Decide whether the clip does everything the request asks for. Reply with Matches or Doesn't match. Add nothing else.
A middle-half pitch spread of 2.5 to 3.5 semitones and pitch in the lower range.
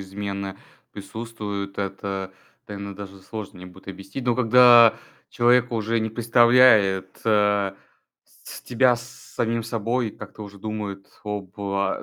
Matches